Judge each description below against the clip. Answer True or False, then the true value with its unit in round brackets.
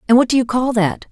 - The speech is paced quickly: True (325 wpm)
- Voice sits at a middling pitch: False (240 Hz)